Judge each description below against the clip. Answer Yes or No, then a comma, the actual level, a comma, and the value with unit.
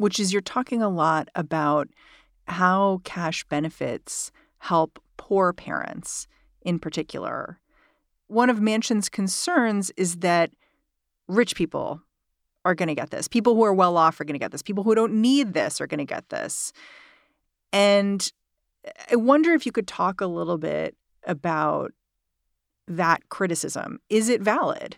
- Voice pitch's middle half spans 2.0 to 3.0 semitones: No, average, 5.2 semitones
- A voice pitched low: No, high, 195 Hz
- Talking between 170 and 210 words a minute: No, average, 155 wpm